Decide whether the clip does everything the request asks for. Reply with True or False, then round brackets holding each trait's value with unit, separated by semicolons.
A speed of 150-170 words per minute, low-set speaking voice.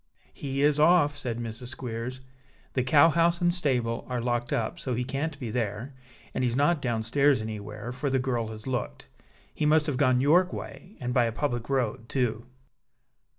False (190 wpm; 130 Hz)